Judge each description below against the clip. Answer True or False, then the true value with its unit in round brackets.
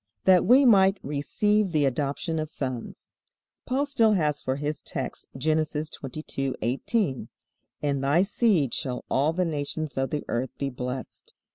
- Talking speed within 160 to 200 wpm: False (145 wpm)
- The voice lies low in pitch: False (150 Hz)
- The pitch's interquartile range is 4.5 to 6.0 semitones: True (5.4 semitones)